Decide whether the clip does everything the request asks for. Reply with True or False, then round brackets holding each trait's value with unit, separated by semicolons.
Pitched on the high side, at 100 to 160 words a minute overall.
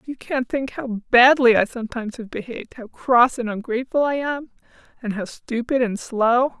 False (245 Hz; 175 wpm)